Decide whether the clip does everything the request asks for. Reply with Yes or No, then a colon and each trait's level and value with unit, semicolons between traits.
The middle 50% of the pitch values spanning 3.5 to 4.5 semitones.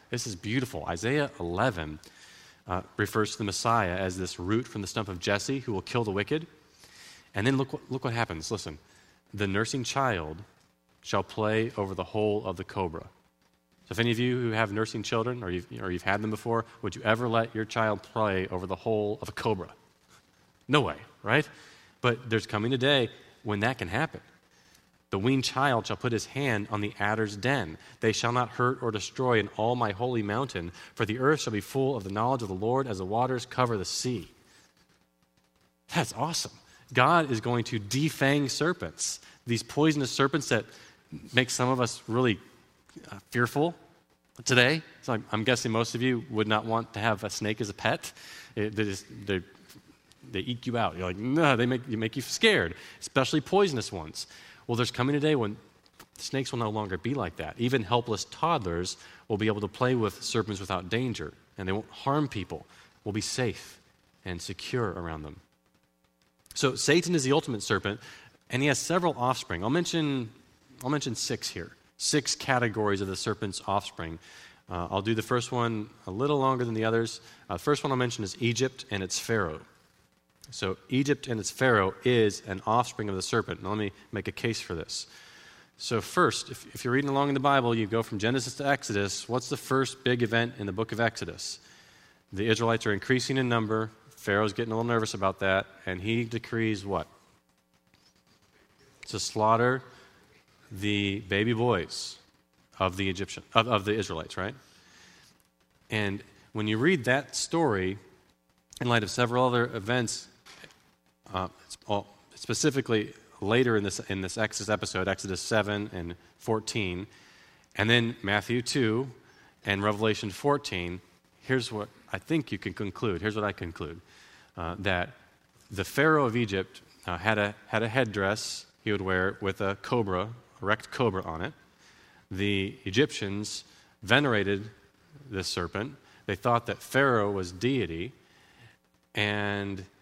Yes: average, 4.2 semitones